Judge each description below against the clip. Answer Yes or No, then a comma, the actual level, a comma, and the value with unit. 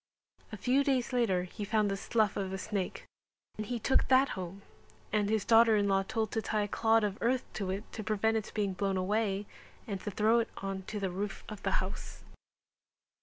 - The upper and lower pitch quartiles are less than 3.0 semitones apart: Yes, narrow, 2.4 semitones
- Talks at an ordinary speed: No, fast, 215 wpm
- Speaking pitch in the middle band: No, high, 210 Hz